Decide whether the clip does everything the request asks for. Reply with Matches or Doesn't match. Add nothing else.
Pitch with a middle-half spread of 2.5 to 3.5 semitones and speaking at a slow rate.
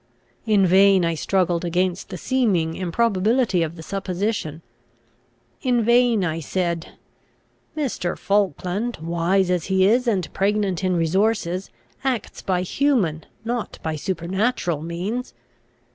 Doesn't match